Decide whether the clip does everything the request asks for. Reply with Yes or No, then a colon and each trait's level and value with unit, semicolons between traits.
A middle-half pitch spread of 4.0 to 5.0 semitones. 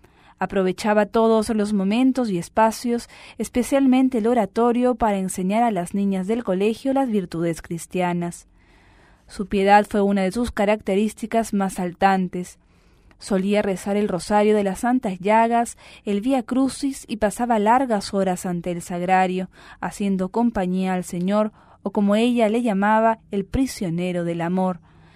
No: average, 3.5 semitones